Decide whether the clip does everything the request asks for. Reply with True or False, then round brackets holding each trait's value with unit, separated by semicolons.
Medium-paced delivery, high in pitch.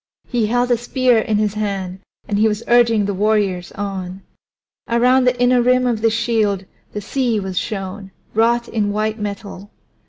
True (175 wpm; 215 Hz)